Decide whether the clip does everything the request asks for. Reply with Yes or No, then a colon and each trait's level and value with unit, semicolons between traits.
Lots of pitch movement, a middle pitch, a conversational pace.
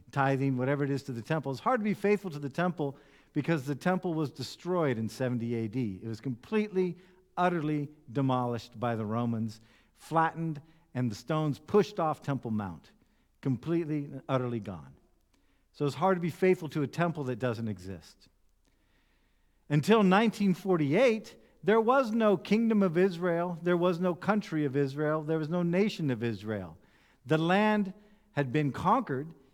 Yes: wide, 6.1 semitones; medium, 150 Hz; average, 160 wpm